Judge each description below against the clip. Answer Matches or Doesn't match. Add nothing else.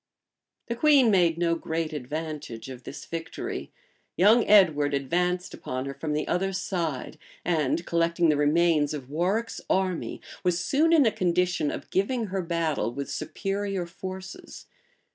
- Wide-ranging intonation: Doesn't match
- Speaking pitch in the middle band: Matches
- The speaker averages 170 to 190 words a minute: Doesn't match